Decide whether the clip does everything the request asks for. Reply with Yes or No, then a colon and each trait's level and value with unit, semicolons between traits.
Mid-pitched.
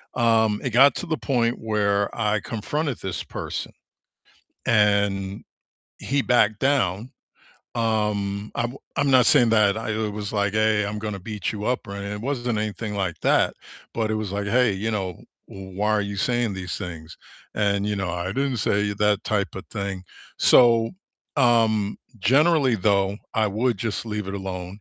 No: low, 105 Hz